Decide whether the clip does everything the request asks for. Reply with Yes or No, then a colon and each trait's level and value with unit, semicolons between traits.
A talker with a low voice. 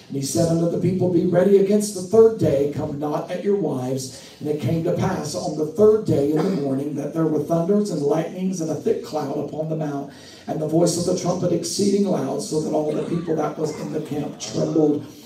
No: medium, 160 Hz